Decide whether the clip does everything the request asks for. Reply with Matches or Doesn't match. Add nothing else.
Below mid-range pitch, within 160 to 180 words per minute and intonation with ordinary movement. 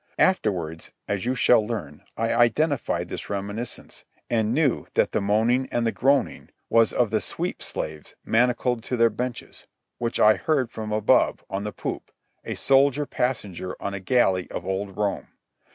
Matches